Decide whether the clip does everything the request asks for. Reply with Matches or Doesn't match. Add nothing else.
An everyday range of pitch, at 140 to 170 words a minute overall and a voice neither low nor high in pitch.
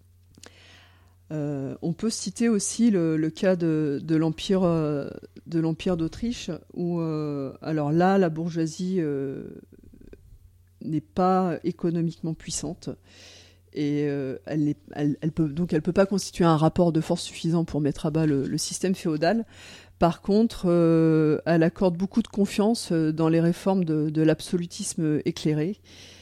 Matches